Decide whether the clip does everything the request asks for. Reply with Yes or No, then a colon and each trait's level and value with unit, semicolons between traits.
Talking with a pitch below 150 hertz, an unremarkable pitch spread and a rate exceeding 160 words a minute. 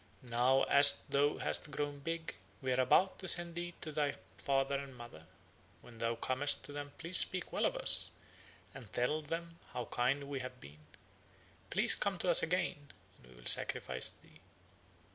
Yes: medium, 140 Hz; average, 4.5 semitones; average, 180 wpm